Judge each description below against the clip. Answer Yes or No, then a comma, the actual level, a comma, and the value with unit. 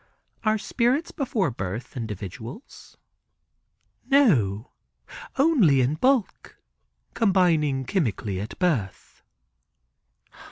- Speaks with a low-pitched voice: No, medium, 150 Hz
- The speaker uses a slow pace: Yes, slow, 75 wpm